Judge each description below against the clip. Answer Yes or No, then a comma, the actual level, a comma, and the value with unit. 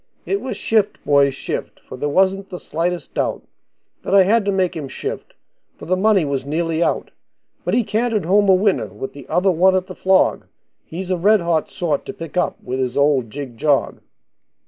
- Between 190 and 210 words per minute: Yes, fast, 205 wpm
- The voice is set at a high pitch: No, medium, 180 Hz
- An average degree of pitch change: Yes, average, 5.0 semitones